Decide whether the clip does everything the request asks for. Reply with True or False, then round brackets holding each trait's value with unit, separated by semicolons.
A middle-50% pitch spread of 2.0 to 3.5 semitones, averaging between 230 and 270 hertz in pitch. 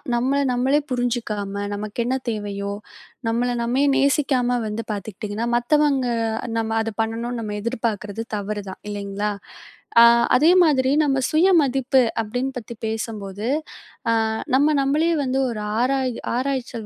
False (4.0 semitones; 240 Hz)